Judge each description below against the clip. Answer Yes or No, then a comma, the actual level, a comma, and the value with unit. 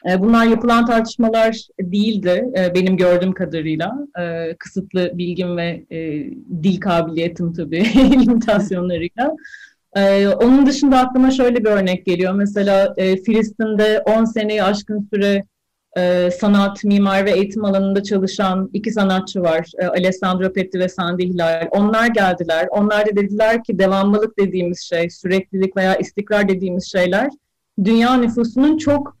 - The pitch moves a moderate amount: Yes, average, 3.4 semitones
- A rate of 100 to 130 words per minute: Yes, average, 120 wpm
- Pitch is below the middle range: No, high, 195 Hz